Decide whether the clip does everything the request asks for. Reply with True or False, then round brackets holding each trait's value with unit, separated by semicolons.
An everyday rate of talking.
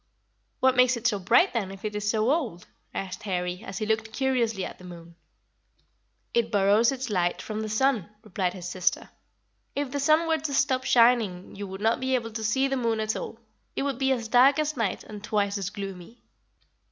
False (210 wpm)